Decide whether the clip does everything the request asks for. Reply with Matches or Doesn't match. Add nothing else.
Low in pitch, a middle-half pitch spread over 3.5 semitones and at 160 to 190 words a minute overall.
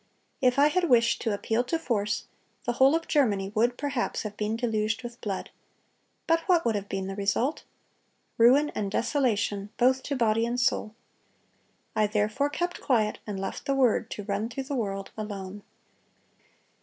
Doesn't match